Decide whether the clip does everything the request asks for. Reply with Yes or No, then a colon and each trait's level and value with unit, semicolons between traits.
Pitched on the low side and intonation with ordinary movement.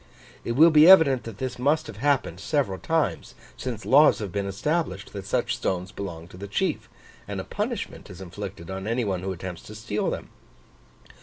No: low, 105 Hz; wide, 6.5 semitones